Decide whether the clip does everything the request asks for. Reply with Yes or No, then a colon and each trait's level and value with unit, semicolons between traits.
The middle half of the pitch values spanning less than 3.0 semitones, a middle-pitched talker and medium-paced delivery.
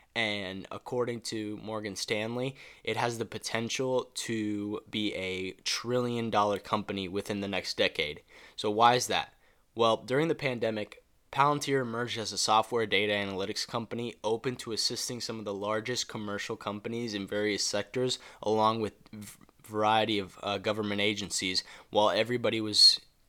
No: narrow, 2.5 semitones; low, 110 Hz; average, 150 wpm